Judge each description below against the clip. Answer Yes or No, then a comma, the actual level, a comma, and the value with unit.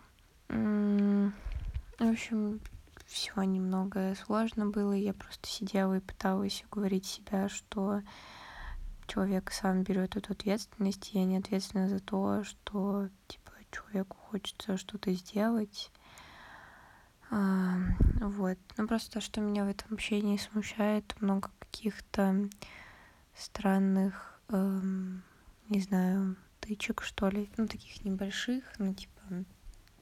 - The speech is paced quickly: No, average, 115 wpm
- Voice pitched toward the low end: No, high, 195 Hz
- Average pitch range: No, narrow, 1.6 semitones